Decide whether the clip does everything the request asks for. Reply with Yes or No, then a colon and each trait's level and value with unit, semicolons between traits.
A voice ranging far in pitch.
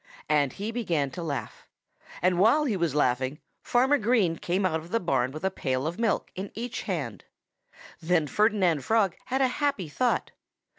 Yes: wide, 6.8 semitones